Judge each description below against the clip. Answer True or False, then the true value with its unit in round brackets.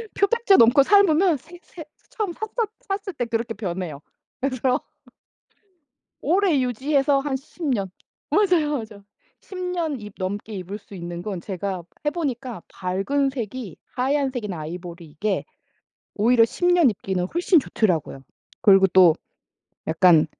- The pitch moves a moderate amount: False (8.6 semitones)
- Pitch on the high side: True (240 Hz)